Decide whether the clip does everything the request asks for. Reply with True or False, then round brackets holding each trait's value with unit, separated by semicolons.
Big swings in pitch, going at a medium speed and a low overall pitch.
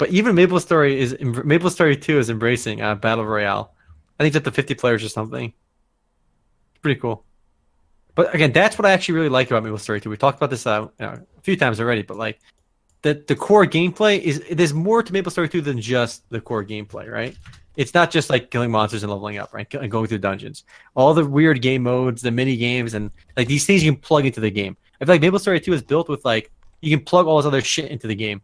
False (6.5 semitones; 250 wpm; 130 Hz)